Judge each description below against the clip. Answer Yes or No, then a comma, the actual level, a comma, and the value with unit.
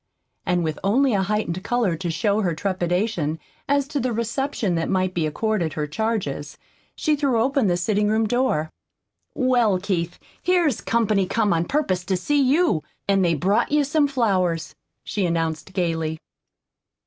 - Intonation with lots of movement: Yes, wide, 6.0 semitones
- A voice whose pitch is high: Yes, high, 200 Hz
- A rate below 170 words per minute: Yes, average, 160 wpm